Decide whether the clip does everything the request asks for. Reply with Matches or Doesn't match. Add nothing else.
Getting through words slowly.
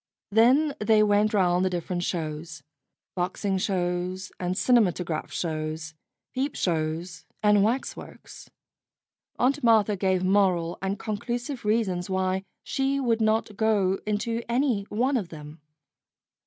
Matches